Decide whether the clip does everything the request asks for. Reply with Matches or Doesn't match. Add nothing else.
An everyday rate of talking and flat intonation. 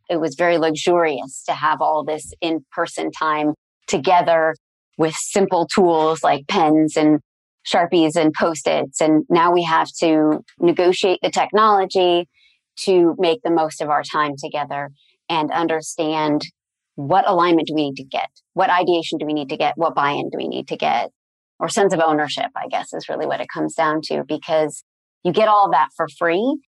Matches